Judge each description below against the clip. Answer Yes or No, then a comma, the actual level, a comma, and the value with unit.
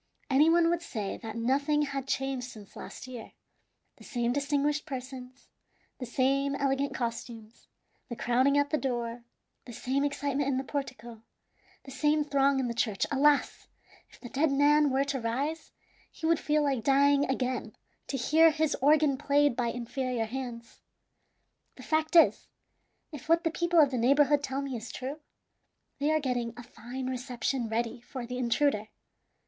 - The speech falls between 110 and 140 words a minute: No, average, 165 wpm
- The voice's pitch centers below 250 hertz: No, very high, 270 Hz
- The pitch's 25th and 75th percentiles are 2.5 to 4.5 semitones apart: Yes, average, 2.9 semitones